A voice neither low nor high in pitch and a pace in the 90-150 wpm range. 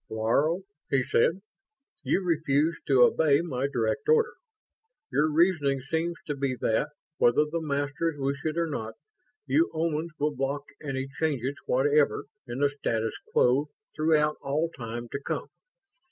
Yes: medium, 145 Hz; average, 145 wpm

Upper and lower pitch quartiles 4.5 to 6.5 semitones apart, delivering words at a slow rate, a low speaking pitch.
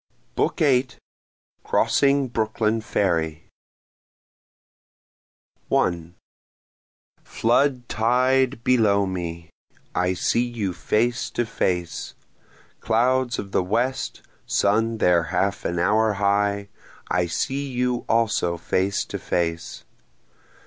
Yes: average, 5.3 semitones; slow, 95 wpm; low, 110 Hz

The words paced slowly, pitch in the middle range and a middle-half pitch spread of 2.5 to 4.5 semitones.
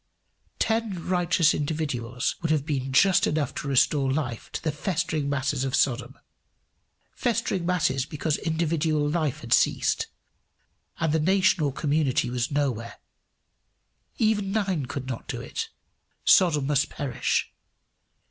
Yes: slow, 130 wpm; medium, 150 Hz; average, 4.0 semitones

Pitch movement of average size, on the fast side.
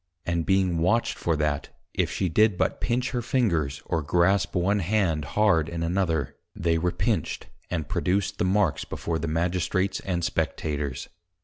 No: average, 3.4 semitones; average, 165 wpm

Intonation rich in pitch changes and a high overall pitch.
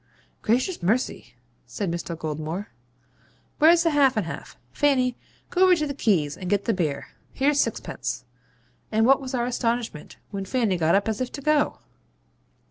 Yes: wide, 7.1 semitones; high, 230 Hz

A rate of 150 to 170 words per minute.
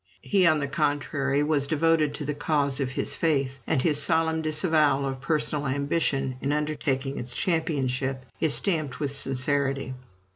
Yes: average, 155 wpm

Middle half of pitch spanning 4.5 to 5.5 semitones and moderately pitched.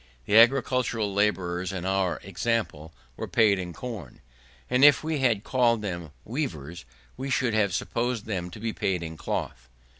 No: average, 5.2 semitones; low, 105 Hz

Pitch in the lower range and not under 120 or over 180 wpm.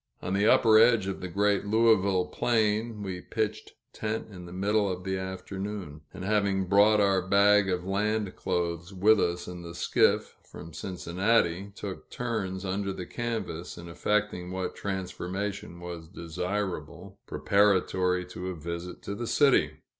Yes: very low, 95 Hz; average, 155 wpm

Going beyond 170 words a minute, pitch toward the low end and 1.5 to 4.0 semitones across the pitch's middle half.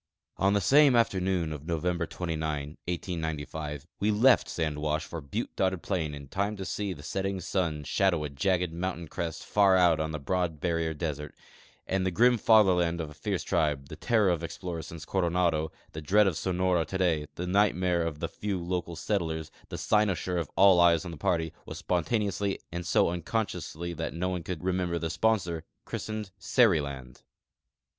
Yes: average, 180 wpm; very low, 85 Hz; average, 3.1 semitones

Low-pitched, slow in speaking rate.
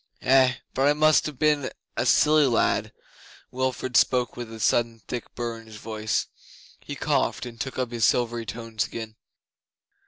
No: low, 120 Hz; average, 165 wpm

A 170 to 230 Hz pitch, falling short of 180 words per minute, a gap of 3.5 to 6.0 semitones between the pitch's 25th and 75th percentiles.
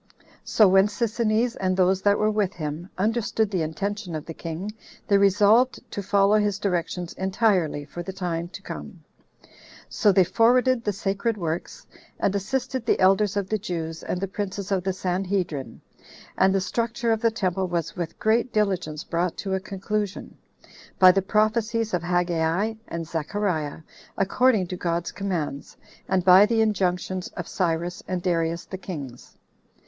No: high, 190 Hz; average, 165 wpm; average, 3.1 semitones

